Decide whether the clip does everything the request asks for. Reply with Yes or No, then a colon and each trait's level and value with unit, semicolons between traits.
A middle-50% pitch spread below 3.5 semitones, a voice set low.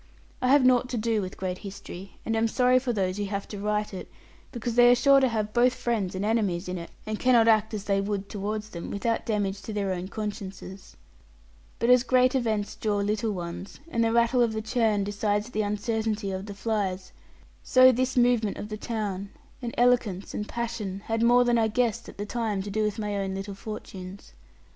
No: average, 2.9 semitones; high, 215 Hz